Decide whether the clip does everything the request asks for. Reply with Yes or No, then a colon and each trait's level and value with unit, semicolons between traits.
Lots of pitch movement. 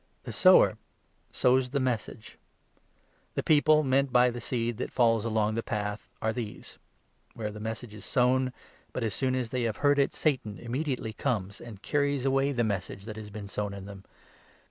No: average, 3.6 semitones